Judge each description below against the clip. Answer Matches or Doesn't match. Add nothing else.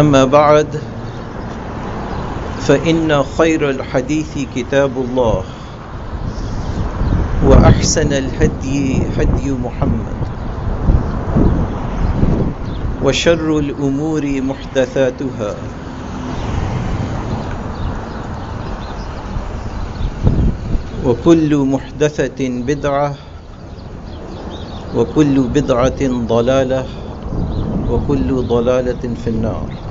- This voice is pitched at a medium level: Doesn't match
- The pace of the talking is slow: Matches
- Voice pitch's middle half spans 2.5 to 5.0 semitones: Matches